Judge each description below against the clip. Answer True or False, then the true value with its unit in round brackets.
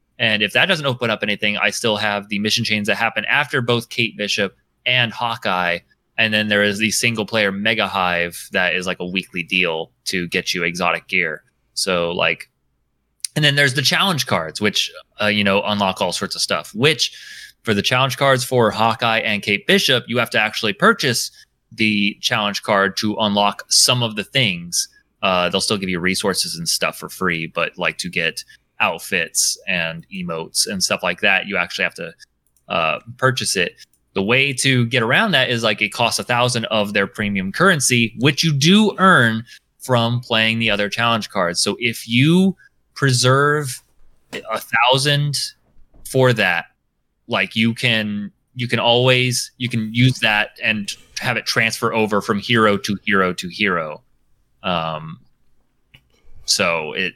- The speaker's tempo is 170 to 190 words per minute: True (175 wpm)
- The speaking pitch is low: True (115 Hz)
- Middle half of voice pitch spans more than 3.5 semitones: True (3.9 semitones)